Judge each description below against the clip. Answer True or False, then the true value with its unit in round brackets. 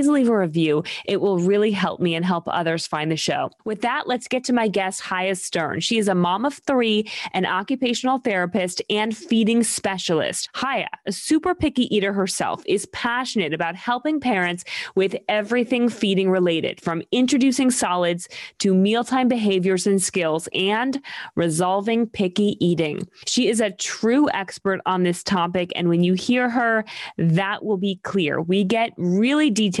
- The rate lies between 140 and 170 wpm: True (165 wpm)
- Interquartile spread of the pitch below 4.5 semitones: False (5.0 semitones)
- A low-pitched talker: False (205 Hz)